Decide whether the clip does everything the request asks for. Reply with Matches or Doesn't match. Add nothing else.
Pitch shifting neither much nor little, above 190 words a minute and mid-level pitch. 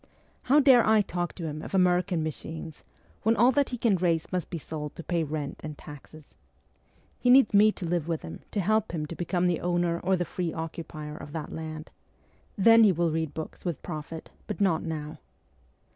Matches